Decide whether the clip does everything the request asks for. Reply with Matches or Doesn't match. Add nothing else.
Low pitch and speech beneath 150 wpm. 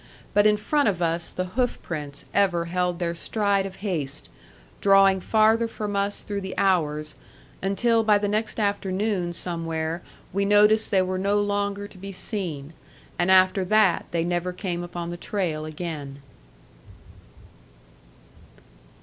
Doesn't match